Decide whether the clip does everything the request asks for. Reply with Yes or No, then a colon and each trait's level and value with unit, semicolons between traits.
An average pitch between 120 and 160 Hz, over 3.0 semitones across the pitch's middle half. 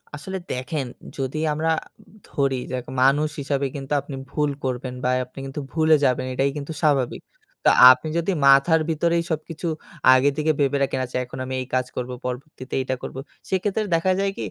Yes: medium, 140 Hz; average, 3.5 semitones